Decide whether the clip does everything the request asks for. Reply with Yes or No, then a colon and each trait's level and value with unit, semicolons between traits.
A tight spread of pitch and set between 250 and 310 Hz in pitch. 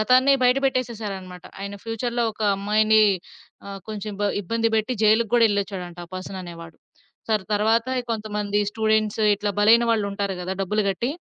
No: narrow, 2.3 semitones; high, 210 Hz